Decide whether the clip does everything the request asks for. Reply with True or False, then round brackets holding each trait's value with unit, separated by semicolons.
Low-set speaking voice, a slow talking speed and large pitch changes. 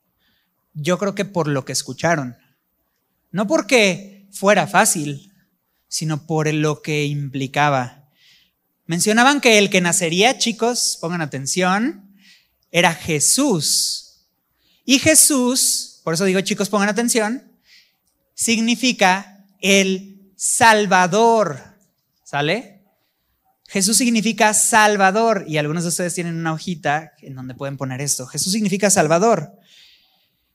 False (185 Hz; 110 wpm; 6.3 semitones)